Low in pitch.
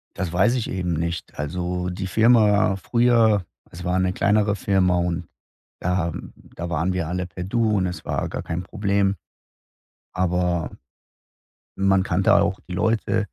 Yes: very low, 95 Hz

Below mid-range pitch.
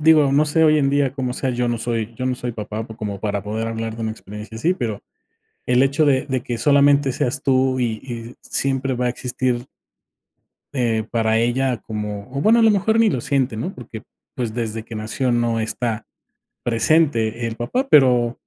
Yes: low, 120 Hz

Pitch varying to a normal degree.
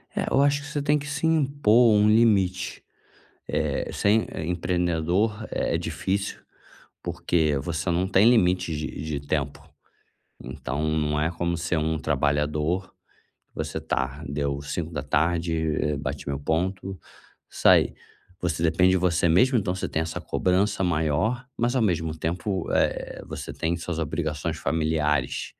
Yes: average, 4.1 semitones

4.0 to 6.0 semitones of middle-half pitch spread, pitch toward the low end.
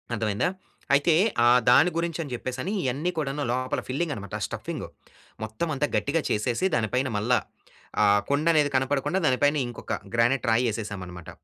Yes: average, 4.4 semitones; low, 130 Hz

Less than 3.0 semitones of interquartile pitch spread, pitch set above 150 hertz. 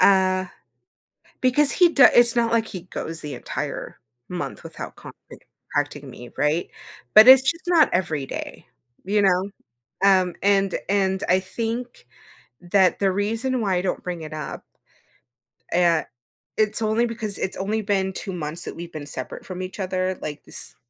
No: average, 3.9 semitones; high, 190 Hz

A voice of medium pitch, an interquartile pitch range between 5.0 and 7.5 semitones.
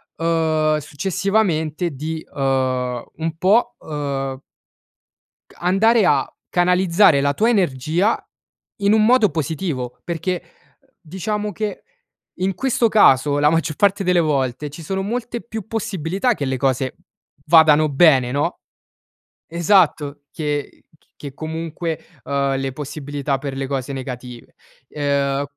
Yes: medium, 155 Hz; average, 5.3 semitones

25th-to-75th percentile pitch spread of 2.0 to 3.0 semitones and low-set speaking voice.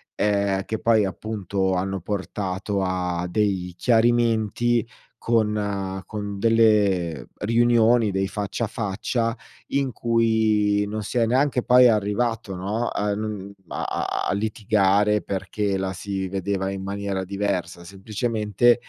Yes: average, 2.7 semitones; low, 105 Hz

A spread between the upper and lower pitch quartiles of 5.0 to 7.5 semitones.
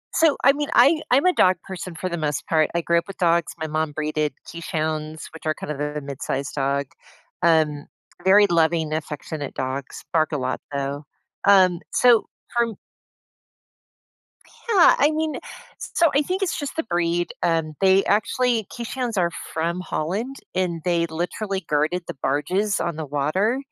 Yes: average, 5.3 semitones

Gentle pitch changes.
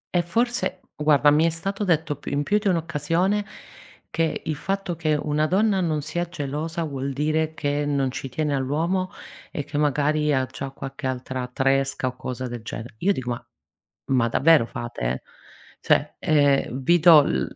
No: average, 3.7 semitones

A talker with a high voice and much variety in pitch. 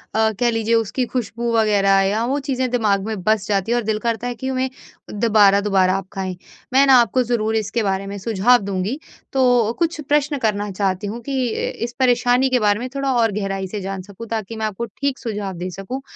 No: high, 220 Hz; average, 3.6 semitones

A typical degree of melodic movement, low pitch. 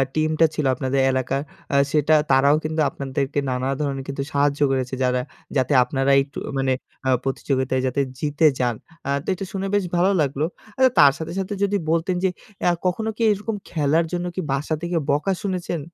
No: average, 4.4 semitones; medium, 145 Hz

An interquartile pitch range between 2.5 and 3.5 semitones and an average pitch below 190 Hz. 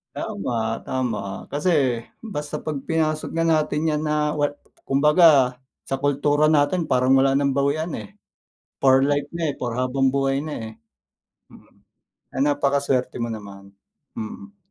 Yes: average, 3.0 semitones; medium, 140 Hz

